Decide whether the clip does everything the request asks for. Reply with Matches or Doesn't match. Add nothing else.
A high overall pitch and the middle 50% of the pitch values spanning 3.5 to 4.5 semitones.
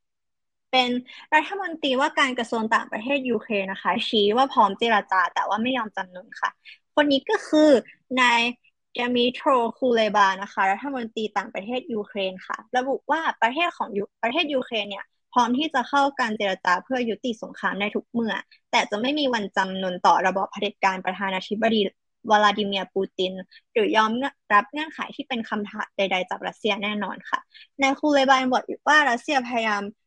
Doesn't match